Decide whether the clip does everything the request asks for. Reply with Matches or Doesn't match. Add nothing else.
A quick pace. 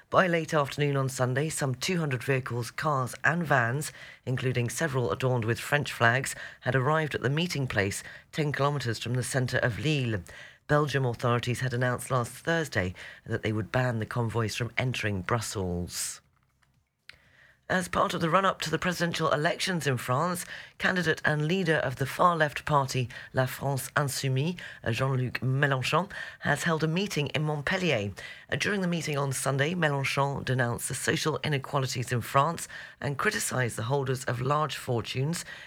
Doesn't match